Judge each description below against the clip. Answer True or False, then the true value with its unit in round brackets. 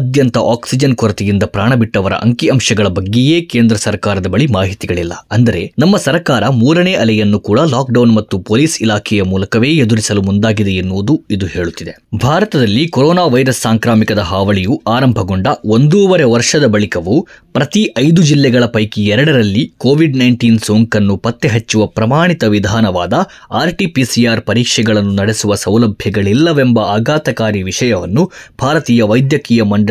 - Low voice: True (115 Hz)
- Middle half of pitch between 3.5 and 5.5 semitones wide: True (3.9 semitones)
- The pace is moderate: False (115 wpm)